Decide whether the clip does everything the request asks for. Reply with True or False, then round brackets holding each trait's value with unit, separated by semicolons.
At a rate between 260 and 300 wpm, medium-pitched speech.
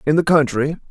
False (200 wpm; 150 Hz)